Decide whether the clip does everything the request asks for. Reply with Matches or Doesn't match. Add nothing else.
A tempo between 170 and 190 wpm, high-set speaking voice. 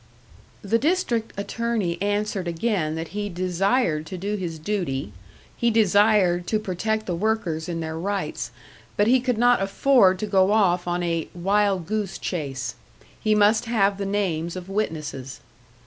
Doesn't match